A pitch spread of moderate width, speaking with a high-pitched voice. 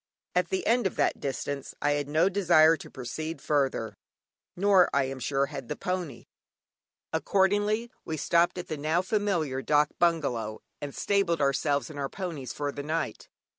No: average, 4.5 semitones; medium, 155 Hz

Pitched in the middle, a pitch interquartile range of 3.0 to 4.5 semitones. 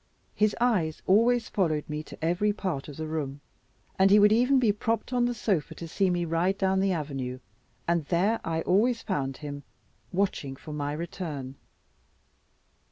No: medium, 175 Hz; wide, 5.5 semitones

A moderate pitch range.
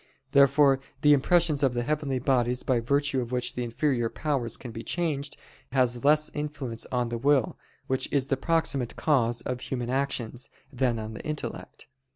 Yes: average, 3.1 semitones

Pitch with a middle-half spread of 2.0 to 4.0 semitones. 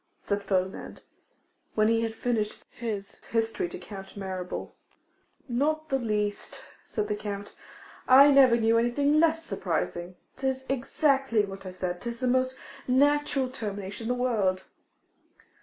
No: average, 4.6 semitones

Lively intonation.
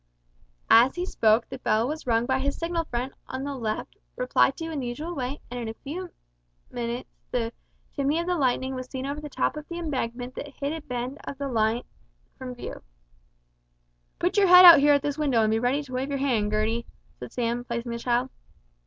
No: average, 3.5 semitones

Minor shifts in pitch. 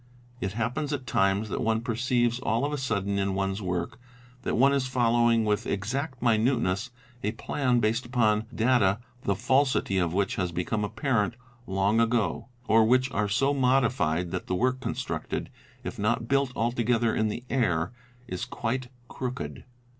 No: average, 3.9 semitones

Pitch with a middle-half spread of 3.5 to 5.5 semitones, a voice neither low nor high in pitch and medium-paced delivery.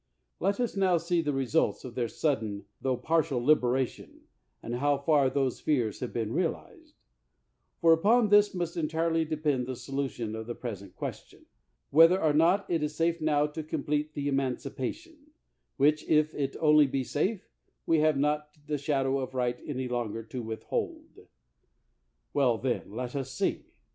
Yes: average, 4.2 semitones; medium, 145 Hz; average, 170 wpm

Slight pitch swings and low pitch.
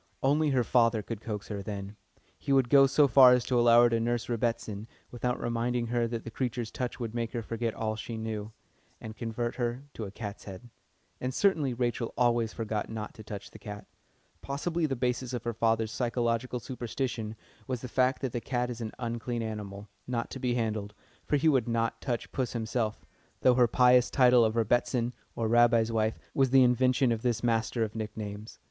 Yes: narrow, 2.0 semitones; low, 120 Hz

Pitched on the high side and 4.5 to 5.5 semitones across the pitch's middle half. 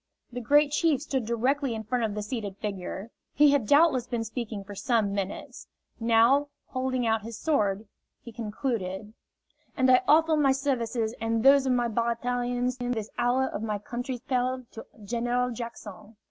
No: high, 240 Hz; average, 2.9 semitones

